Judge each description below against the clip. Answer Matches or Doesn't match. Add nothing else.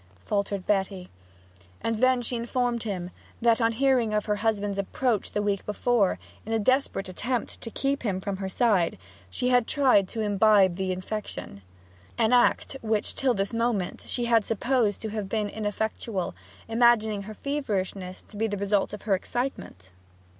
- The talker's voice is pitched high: Matches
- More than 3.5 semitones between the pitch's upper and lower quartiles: Doesn't match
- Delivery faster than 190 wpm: Doesn't match